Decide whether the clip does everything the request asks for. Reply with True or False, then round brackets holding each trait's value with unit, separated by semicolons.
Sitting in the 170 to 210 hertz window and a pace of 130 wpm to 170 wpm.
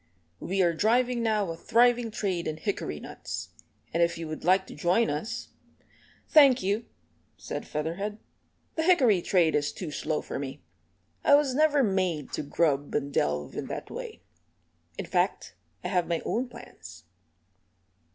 True (185 Hz; 160 wpm)